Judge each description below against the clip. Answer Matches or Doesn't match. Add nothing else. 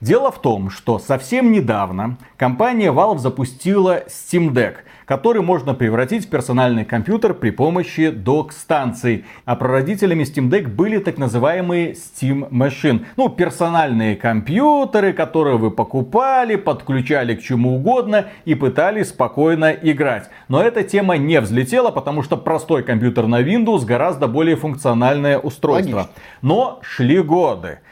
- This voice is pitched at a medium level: Matches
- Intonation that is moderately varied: Doesn't match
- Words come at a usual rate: Matches